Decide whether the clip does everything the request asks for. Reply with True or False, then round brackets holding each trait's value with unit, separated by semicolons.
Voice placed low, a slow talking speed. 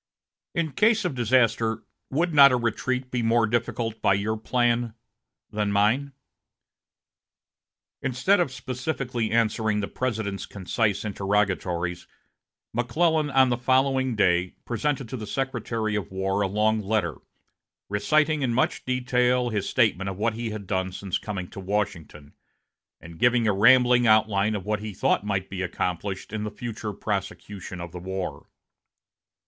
False (110 Hz; 145 wpm)